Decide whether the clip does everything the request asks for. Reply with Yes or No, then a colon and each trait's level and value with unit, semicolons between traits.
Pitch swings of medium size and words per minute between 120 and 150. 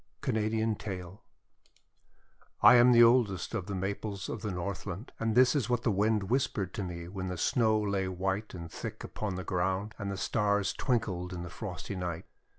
No: average, 3.3 semitones; average, 185 wpm